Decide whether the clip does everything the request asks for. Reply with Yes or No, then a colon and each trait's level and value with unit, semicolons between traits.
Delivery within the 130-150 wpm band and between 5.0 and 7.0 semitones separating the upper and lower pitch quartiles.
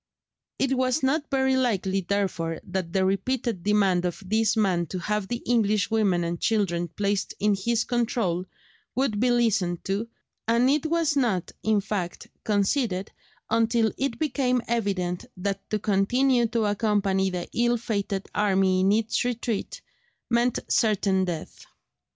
No: average, 145 wpm; average, 3.9 semitones